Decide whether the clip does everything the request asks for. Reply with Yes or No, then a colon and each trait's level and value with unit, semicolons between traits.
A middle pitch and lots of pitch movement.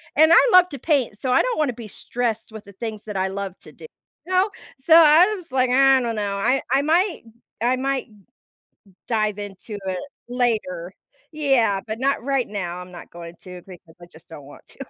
No: high, 230 Hz; wide, 5.8 semitones